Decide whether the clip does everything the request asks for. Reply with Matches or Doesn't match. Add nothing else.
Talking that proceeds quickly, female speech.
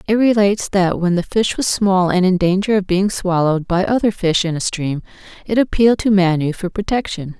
Matches